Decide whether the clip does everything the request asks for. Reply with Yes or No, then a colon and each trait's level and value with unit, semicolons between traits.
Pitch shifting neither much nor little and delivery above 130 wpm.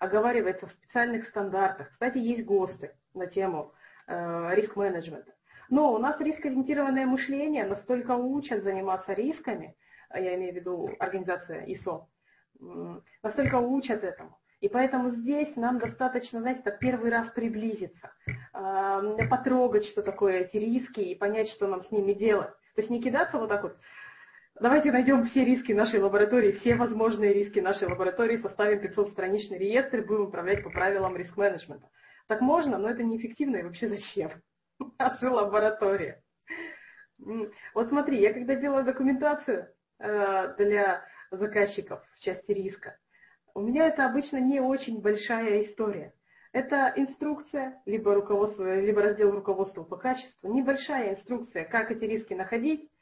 Yes: average, 4.5 semitones; average, 145 wpm